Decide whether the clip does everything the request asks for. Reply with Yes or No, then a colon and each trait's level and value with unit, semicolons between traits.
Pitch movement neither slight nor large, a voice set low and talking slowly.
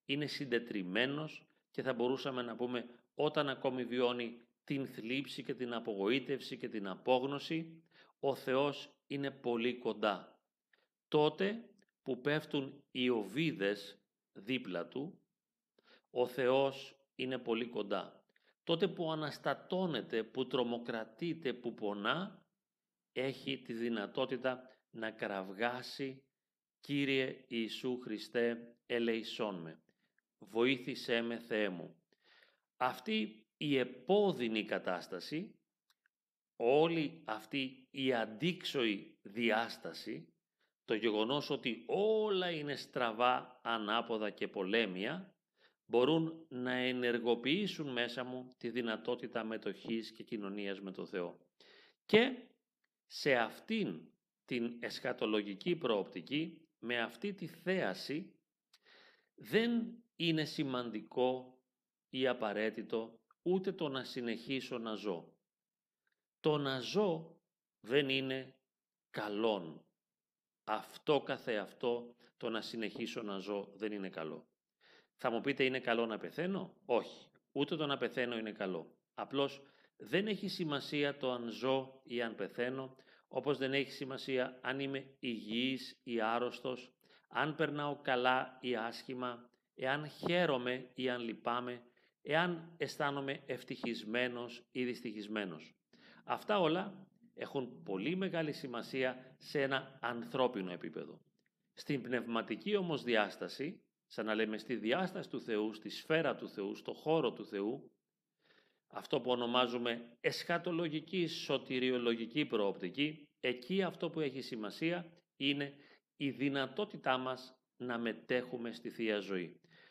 Yes: average, 4.1 semitones; low, 130 Hz; slow, 110 wpm